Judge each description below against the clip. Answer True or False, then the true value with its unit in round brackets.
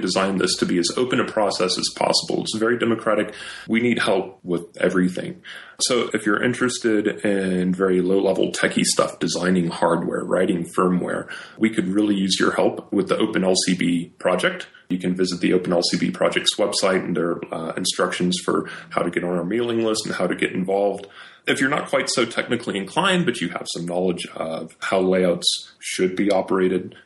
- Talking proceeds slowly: False (185 wpm)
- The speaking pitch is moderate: False (95 Hz)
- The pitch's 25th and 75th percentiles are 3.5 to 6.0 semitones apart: False (2.7 semitones)